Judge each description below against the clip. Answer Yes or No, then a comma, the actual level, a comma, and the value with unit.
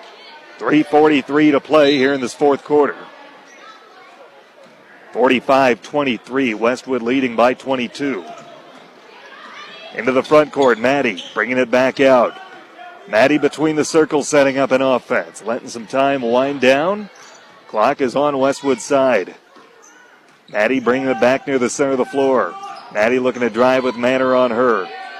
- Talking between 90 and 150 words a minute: Yes, average, 140 wpm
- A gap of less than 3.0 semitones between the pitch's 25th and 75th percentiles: Yes, narrow, 2.4 semitones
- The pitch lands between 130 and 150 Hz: Yes, low, 135 Hz